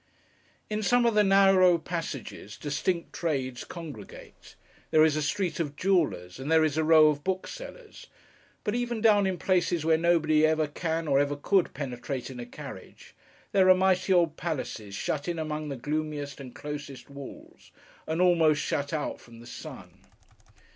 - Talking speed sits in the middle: Yes, average, 170 wpm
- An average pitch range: Yes, average, 4.3 semitones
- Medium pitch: Yes, medium, 155 Hz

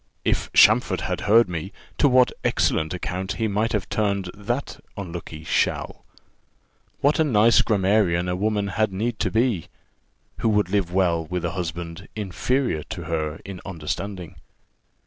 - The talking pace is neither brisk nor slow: Yes, average, 150 wpm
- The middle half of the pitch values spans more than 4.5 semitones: No, average, 3.8 semitones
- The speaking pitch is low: Yes, very low, 95 Hz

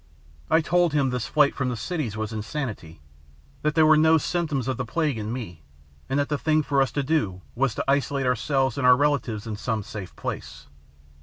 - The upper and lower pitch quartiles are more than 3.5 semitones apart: Yes, average, 5.1 semitones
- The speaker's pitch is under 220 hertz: Yes, low, 135 Hz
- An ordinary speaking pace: No, fast, 210 wpm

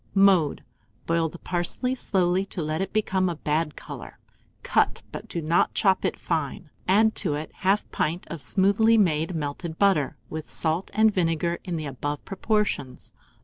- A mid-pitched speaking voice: Yes, medium, 175 Hz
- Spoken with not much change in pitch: No, average, 3.8 semitones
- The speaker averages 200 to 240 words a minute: No, average, 165 wpm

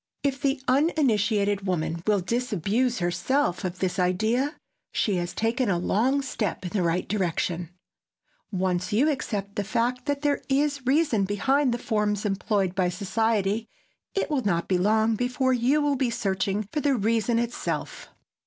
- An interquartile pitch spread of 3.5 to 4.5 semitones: No, average, 5.3 semitones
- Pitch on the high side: Yes, high, 220 Hz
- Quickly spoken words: No, average, 160 wpm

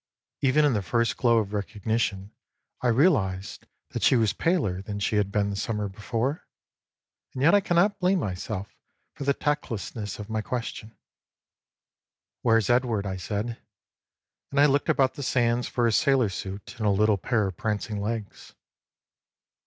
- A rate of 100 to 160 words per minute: No, average, 170 wpm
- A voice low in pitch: Yes, low, 110 Hz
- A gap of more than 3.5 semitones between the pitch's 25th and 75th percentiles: Yes, average, 4.1 semitones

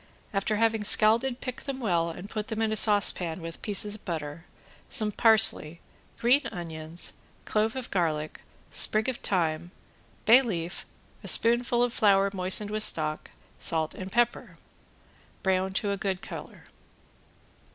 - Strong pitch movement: No, average, 4.5 semitones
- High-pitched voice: Yes, high, 205 Hz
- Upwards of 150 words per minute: No, average, 145 wpm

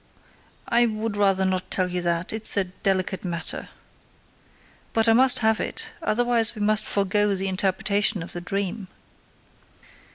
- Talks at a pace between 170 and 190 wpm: No, average, 155 wpm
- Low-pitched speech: No, high, 200 Hz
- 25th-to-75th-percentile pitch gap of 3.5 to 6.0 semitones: No, average, 2.9 semitones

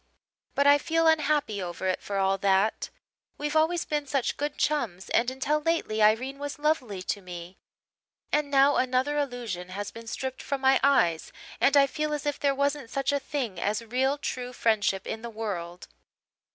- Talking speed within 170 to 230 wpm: Yes, average, 180 wpm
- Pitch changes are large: Yes, wide, 5.9 semitones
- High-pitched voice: Yes, very high, 260 Hz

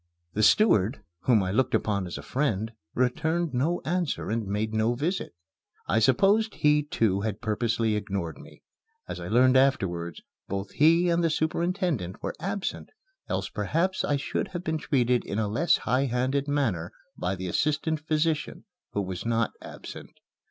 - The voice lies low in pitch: Yes, low, 125 Hz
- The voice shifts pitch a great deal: Yes, wide, 7.1 semitones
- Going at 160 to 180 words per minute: Yes, average, 165 wpm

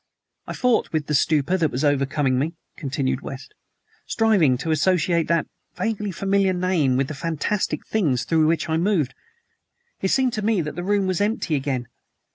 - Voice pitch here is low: No, medium, 165 Hz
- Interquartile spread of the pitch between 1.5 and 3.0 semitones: No, average, 5.3 semitones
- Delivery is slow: No, average, 175 wpm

